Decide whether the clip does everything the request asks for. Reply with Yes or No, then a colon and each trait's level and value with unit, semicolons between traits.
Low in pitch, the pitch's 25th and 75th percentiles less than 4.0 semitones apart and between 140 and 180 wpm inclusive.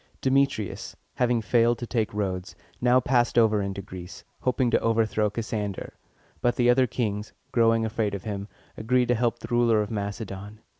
Yes: low, 115 Hz; average, 2.8 semitones; average, 165 wpm